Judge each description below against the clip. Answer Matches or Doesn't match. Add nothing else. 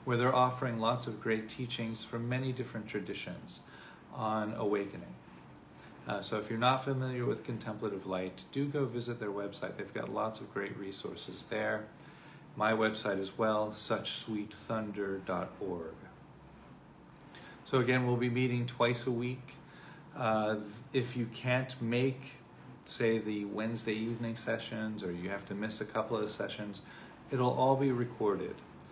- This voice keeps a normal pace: Matches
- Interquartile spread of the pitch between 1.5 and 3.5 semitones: Matches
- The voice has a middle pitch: Doesn't match